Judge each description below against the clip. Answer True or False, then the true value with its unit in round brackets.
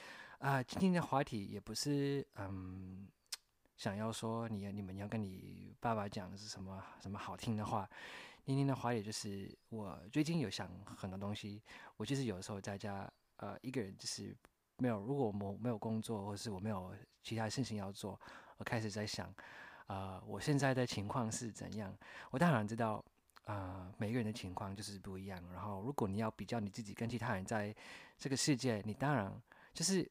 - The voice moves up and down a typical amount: True (3.2 semitones)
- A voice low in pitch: True (110 Hz)